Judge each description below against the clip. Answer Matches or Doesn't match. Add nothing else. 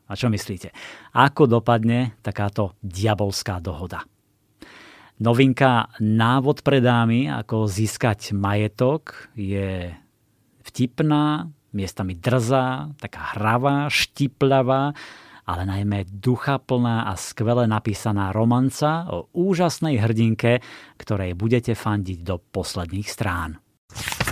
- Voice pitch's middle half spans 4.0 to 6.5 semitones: Matches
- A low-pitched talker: Matches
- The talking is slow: Matches